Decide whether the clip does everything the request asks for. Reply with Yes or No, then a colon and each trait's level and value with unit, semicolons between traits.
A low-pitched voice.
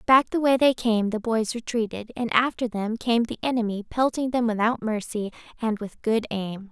No: high, 230 Hz